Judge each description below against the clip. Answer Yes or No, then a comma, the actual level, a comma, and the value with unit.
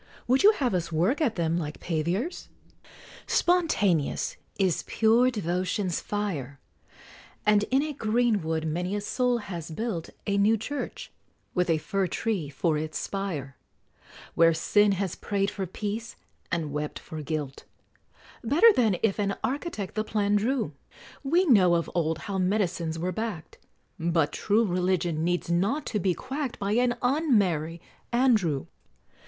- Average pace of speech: Yes, average, 150 wpm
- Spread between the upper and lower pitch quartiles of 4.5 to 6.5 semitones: Yes, average, 5.3 semitones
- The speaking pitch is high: Yes, high, 195 Hz